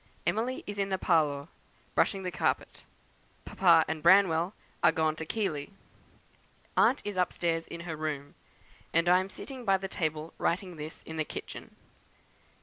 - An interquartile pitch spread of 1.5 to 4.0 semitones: Yes, average, 3.4 semitones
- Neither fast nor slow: Yes, average, 155 wpm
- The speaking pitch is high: No, medium, 170 Hz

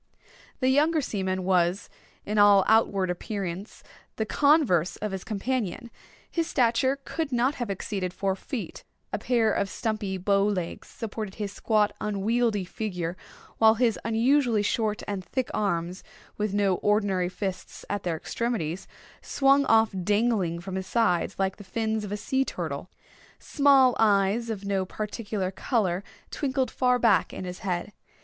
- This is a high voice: Yes, high, 210 Hz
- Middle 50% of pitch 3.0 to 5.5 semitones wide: Yes, average, 3.5 semitones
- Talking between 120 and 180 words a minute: Yes, average, 150 wpm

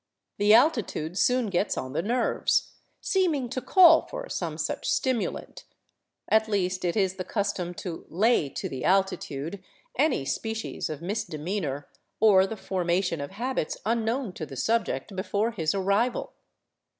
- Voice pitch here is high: Yes, high, 200 Hz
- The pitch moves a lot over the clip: No, average, 4.7 semitones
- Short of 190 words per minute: Yes, average, 155 wpm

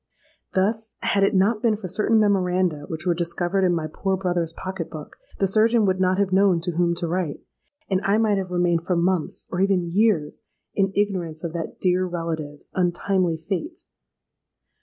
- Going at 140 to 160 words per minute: No, average, 175 wpm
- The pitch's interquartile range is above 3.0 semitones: No, narrow, 2.5 semitones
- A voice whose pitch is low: No, medium, 185 Hz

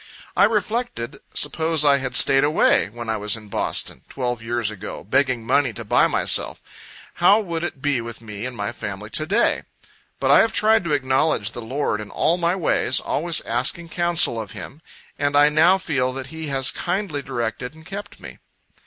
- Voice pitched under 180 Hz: Yes, low, 135 Hz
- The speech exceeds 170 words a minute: Yes, average, 190 wpm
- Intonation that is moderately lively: No, wide, 5.9 semitones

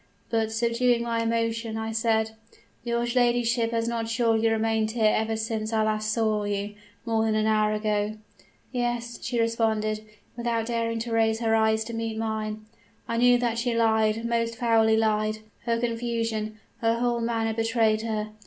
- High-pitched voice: Yes, high, 225 Hz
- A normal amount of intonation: No, narrow, 1.1 semitones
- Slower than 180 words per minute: Yes, average, 165 wpm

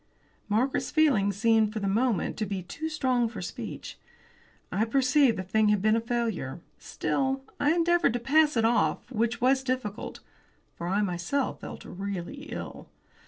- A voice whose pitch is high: Yes, high, 230 Hz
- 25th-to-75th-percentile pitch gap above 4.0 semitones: Yes, average, 4.7 semitones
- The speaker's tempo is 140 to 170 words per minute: Yes, average, 165 wpm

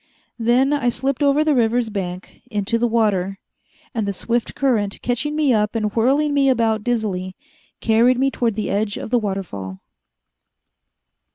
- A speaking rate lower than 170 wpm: Yes, average, 160 wpm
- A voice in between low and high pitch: No, high, 230 Hz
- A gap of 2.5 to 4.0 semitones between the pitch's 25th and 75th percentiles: Yes, average, 3.7 semitones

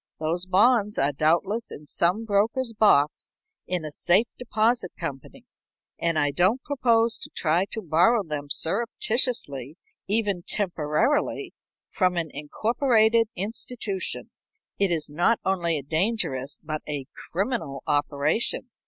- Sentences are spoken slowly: Yes, slow, 125 wpm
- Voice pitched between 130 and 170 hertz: No, medium, 185 Hz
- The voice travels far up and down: Yes, wide, 6.6 semitones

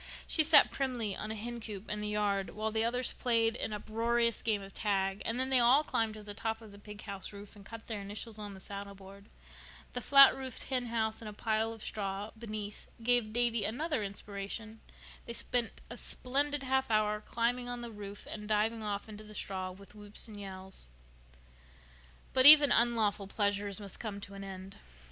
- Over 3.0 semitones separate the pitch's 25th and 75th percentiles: No, average, 2.7 semitones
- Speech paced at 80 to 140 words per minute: No, average, 195 wpm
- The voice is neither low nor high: No, high, 215 Hz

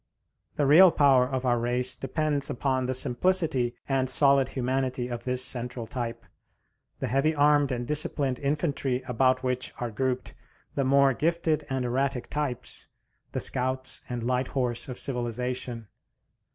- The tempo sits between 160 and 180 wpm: No, average, 145 wpm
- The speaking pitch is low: Yes, low, 130 Hz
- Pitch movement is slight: Yes, narrow, 2.0 semitones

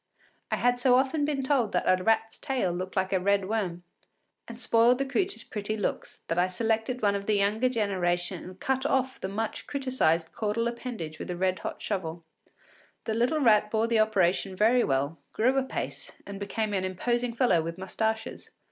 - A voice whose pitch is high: Yes, high, 215 Hz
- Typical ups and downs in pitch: Yes, average, 4.7 semitones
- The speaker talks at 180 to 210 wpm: Yes, average, 190 wpm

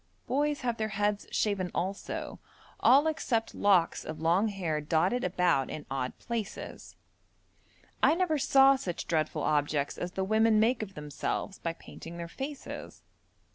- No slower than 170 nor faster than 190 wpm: No, average, 145 wpm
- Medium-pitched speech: No, high, 195 Hz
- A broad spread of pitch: Yes, wide, 6.0 semitones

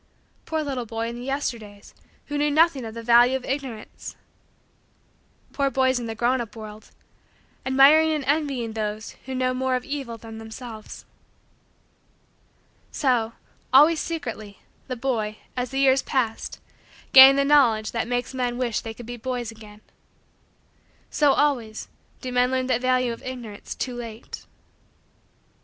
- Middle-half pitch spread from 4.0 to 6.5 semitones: No, average, 3.0 semitones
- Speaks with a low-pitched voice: No, very high, 250 Hz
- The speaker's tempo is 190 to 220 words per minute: No, average, 150 wpm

